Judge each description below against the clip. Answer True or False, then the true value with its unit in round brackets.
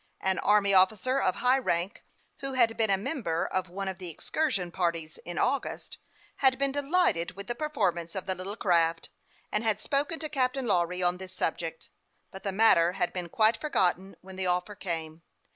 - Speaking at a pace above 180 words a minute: True (190 wpm)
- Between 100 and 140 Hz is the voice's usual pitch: False (190 Hz)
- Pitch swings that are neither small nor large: False (5.9 semitones)